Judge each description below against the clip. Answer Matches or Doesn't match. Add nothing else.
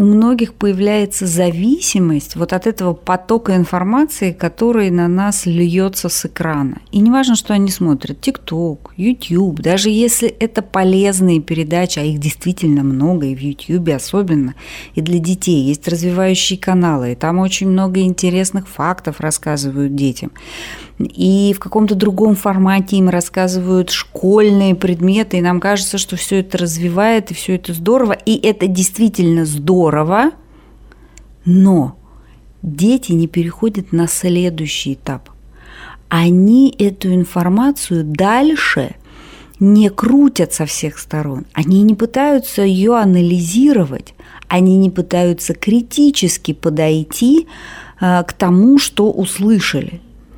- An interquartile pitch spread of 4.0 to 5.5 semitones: Doesn't match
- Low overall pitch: Doesn't match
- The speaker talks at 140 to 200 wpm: Doesn't match